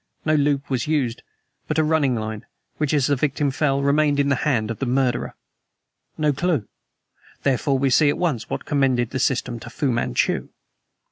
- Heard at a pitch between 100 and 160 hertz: Yes, medium, 140 Hz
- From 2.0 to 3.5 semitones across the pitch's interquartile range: Yes, average, 3.1 semitones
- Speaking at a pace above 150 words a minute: Yes, average, 185 wpm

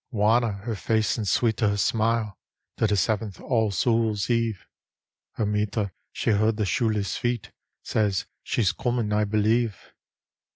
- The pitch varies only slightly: Yes, narrow, 1.9 semitones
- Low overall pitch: Yes, low, 110 Hz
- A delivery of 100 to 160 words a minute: Yes, average, 150 wpm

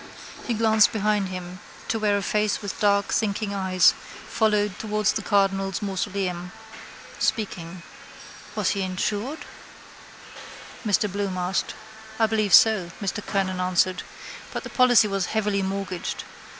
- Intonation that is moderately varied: No, narrow, 2.2 semitones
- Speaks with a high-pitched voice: Yes, high, 200 Hz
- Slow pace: Yes, slow, 130 wpm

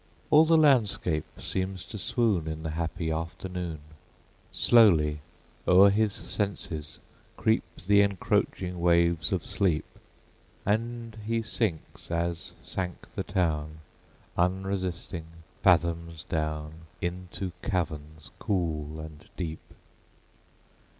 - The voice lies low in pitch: Yes, very low, 85 Hz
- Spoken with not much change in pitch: No, average, 3.8 semitones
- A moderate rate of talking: No, slow, 100 wpm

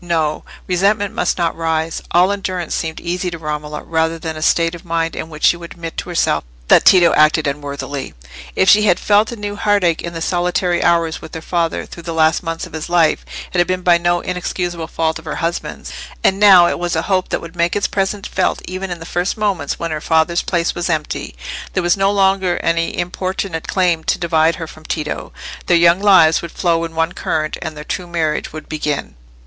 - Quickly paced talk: Yes, fast, 215 wpm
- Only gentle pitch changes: Yes, narrow, 2.1 semitones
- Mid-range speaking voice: Yes, medium, 170 Hz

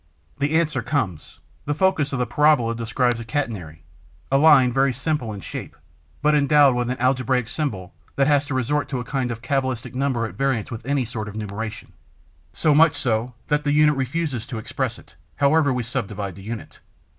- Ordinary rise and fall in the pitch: Yes, average, 4.1 semitones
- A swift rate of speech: No, average, 195 wpm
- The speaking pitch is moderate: No, low, 130 Hz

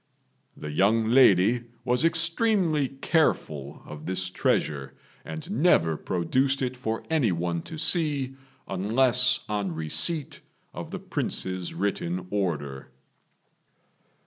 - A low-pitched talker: Yes, low, 110 Hz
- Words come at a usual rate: No, slow, 110 wpm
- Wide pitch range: Yes, wide, 8.1 semitones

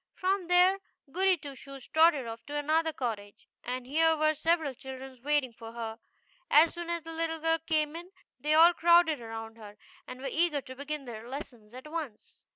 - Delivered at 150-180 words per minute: No, average, 190 wpm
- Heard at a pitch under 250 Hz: No, very high, 295 Hz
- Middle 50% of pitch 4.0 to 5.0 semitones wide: Yes, average, 4.4 semitones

